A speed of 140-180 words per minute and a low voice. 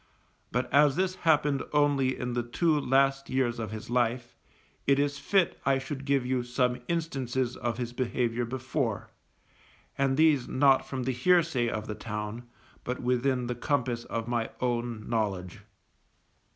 Yes: average, 155 wpm; low, 125 Hz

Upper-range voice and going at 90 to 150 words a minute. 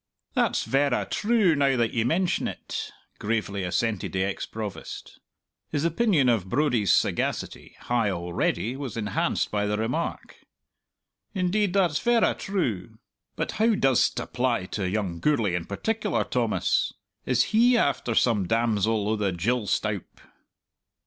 No: low, 120 Hz; slow, 135 wpm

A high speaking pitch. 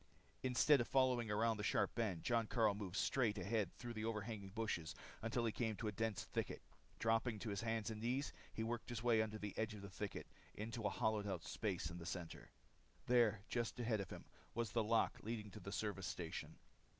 No: low, 110 Hz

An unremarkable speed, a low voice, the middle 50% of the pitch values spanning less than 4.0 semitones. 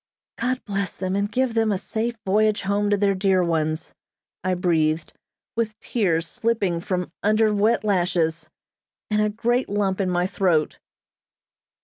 No: average, 150 wpm; high, 200 Hz; average, 3.3 semitones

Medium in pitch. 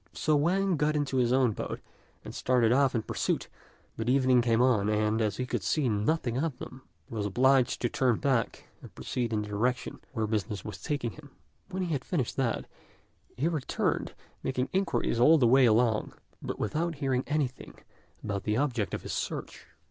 No: low, 125 Hz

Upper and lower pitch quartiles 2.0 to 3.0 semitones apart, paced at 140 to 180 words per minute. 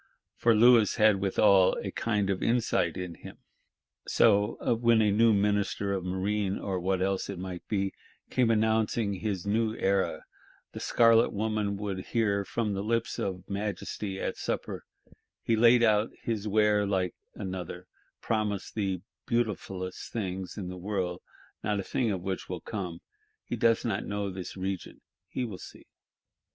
Yes: narrow, 2.6 semitones; average, 160 wpm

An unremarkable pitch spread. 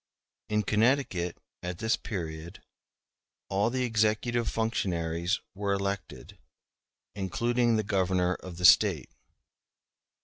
Yes: average, 3.9 semitones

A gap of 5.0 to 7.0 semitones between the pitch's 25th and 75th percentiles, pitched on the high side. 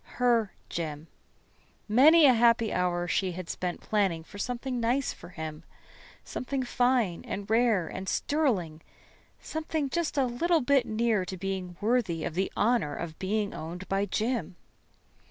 Yes: wide, 5.6 semitones; high, 215 Hz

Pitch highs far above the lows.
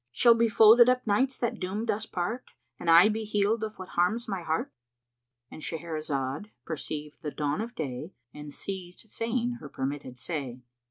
Yes: wide, 6.6 semitones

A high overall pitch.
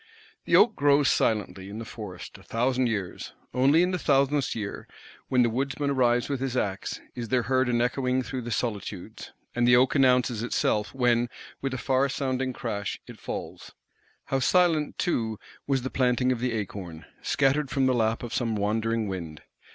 No: low, 125 Hz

